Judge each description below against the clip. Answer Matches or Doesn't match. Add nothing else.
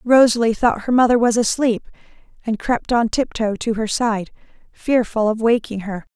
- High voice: Matches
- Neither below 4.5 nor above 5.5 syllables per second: Matches